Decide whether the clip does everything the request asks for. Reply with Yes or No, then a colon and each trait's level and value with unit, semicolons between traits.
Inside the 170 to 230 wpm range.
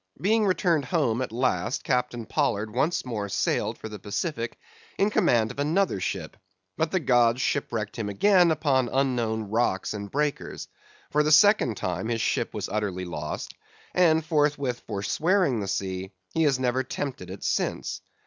No: average, 160 wpm